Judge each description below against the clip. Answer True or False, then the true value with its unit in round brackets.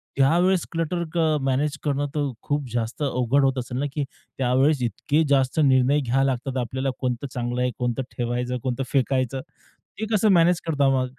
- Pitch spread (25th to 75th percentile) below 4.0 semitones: True (2.7 semitones)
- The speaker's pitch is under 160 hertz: True (135 Hz)